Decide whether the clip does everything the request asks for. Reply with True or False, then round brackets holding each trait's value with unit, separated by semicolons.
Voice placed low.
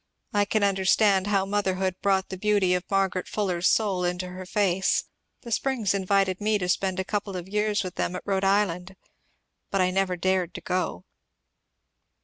False (190 Hz)